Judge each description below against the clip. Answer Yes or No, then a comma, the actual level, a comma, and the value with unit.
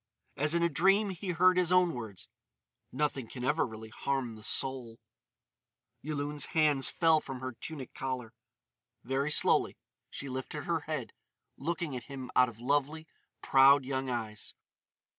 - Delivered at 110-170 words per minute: Yes, average, 150 wpm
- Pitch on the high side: No, low, 135 Hz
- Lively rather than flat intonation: No, average, 3.8 semitones